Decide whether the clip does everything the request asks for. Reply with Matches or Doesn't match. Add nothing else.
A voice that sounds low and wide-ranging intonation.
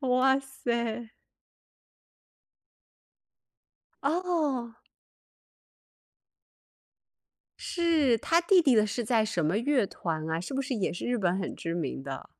Doesn't match